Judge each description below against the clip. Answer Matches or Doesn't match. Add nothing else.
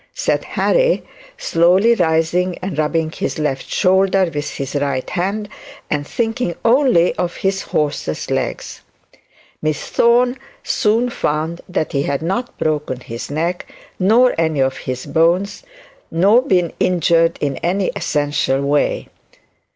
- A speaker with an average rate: Doesn't match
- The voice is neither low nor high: Matches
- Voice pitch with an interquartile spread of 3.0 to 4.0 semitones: Doesn't match